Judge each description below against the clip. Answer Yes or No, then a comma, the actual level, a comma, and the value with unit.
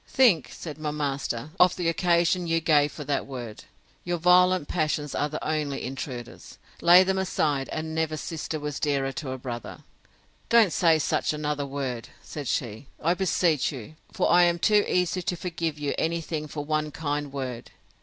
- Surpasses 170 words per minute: Yes, average, 180 wpm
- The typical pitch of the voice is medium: Yes, medium, 155 Hz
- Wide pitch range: No, average, 3.3 semitones